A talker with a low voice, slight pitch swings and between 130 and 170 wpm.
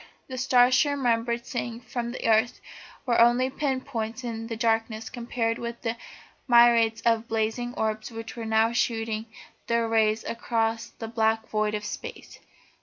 No: high, 230 Hz; narrow, 1.3 semitones; average, 160 wpm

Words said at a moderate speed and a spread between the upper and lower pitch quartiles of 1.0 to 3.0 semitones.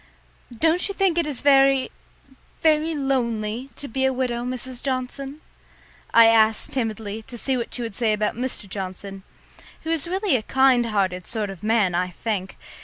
No: average, 175 wpm; average, 4.2 semitones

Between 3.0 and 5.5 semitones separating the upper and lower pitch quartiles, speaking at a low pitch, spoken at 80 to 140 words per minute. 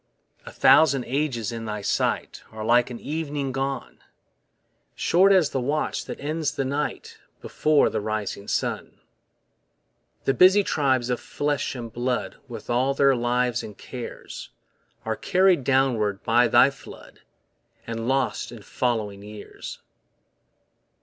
Yes: average, 3.6 semitones; low, 125 Hz; slow, 135 wpm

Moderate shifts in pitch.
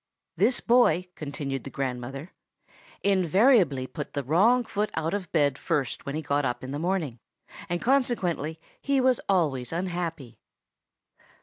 No: wide, 6.0 semitones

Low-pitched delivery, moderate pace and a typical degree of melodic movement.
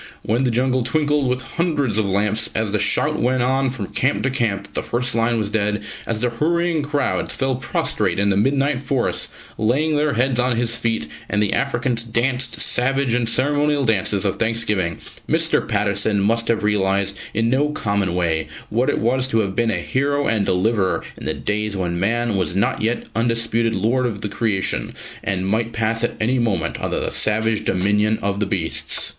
Yes: low, 115 Hz; average, 195 wpm; average, 3.9 semitones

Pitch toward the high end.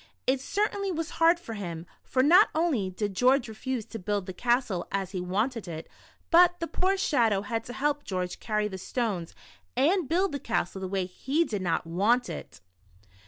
Yes: high, 230 Hz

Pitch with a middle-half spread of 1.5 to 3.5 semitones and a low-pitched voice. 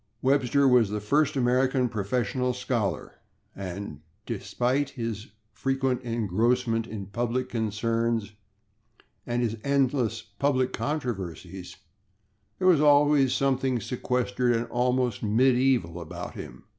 Yes: average, 3.1 semitones; low, 120 Hz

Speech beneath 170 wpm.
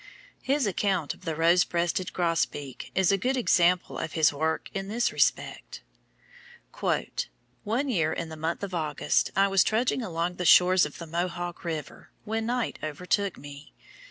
Yes: average, 155 wpm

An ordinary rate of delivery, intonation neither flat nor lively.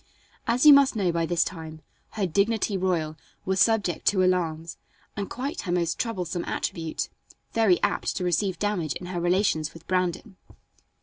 Yes: average, 165 wpm; average, 3.5 semitones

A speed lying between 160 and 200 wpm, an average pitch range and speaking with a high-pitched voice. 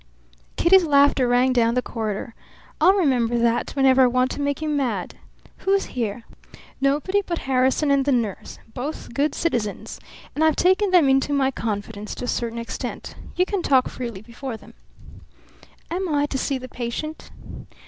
Yes: average, 170 wpm; average, 4.1 semitones; very high, 265 Hz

